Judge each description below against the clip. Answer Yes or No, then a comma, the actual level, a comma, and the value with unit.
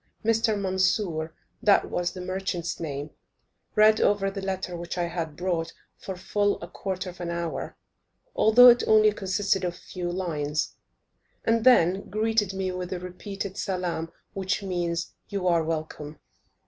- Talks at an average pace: Yes, average, 155 wpm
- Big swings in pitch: No, narrow, 2.6 semitones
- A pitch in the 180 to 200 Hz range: Yes, medium, 185 Hz